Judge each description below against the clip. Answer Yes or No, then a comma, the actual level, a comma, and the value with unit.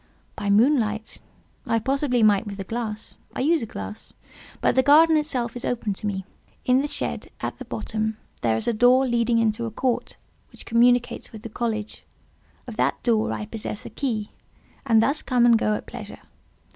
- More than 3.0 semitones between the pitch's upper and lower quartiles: No, average, 2.7 semitones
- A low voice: No, high, 230 Hz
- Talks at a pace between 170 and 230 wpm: Yes, average, 185 wpm